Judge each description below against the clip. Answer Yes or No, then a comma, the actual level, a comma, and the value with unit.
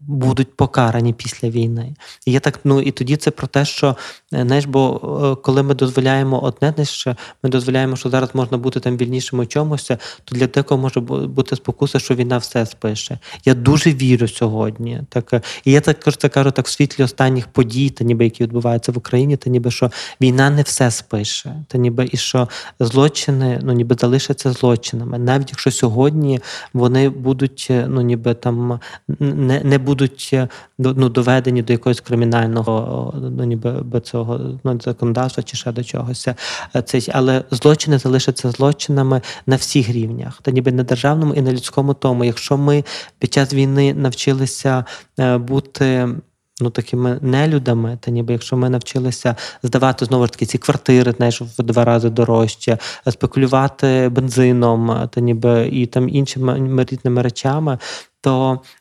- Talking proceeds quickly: Yes, fast, 165 wpm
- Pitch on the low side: Yes, low, 130 Hz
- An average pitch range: No, narrow, 1.9 semitones